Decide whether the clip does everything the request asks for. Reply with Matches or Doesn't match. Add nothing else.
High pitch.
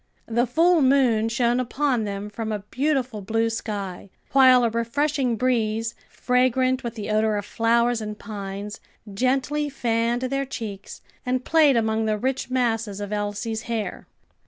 Matches